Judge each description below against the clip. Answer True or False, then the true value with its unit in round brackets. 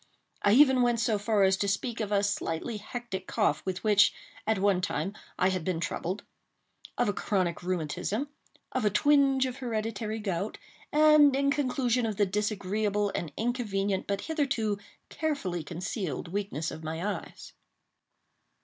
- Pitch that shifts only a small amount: False (4.3 semitones)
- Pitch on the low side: False (210 Hz)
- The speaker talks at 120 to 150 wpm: True (145 wpm)